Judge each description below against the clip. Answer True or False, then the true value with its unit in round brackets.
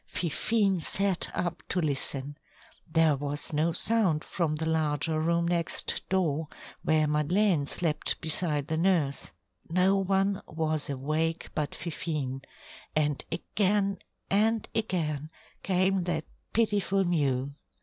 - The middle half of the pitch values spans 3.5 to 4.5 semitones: True (3.9 semitones)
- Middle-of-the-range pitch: True (165 Hz)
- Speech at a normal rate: False (120 wpm)